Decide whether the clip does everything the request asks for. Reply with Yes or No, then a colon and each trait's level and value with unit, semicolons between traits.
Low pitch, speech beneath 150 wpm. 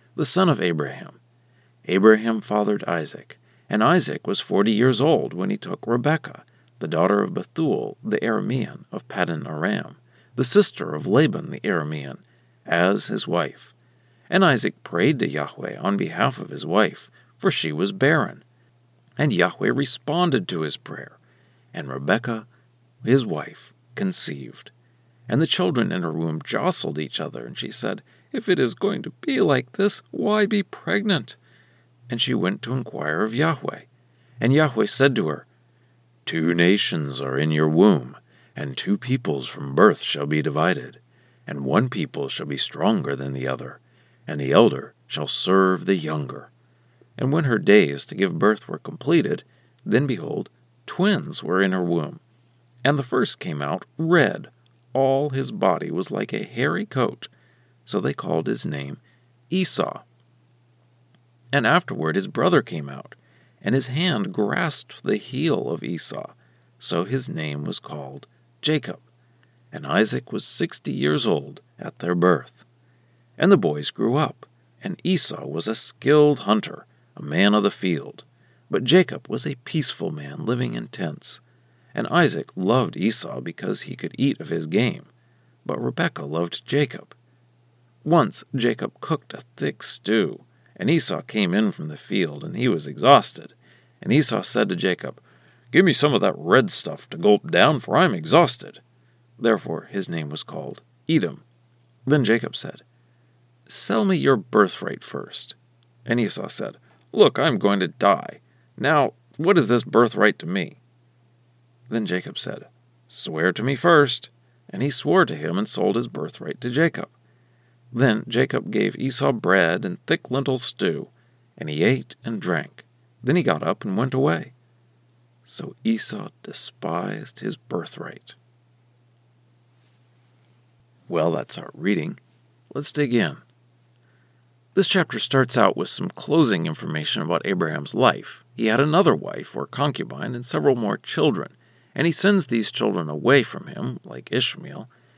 No: low, 120 Hz; average, 155 wpm